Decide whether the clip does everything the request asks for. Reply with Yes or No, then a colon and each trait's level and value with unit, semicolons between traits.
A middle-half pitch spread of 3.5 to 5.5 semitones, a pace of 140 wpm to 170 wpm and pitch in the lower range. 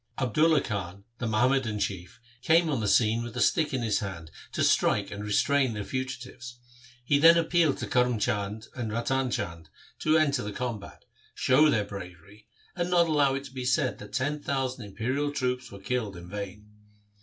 No: average, 5.1 semitones; average, 185 wpm; low, 125 Hz